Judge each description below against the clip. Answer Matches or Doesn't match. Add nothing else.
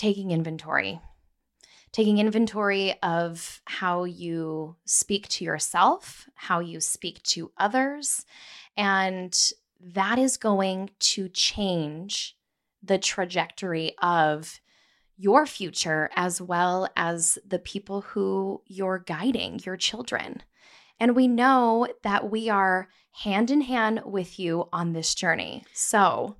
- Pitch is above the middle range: Matches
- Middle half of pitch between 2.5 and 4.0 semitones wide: Matches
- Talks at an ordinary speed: Doesn't match